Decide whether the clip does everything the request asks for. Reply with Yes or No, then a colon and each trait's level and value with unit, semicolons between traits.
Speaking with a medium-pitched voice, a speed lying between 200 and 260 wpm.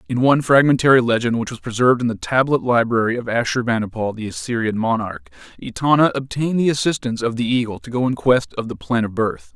No: low, 120 Hz; fast, 205 wpm